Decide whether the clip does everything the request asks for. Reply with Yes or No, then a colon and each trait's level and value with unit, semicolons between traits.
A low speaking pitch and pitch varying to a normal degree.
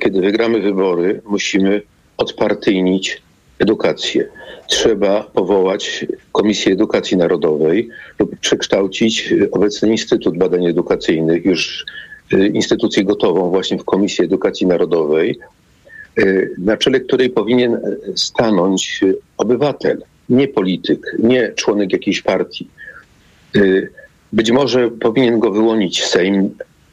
Yes: low, 110 Hz; average, 4.6 semitones